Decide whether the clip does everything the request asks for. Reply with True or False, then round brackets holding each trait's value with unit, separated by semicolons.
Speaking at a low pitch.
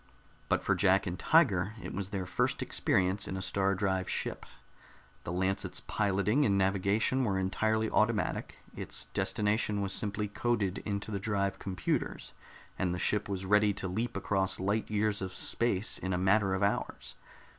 True (100 Hz)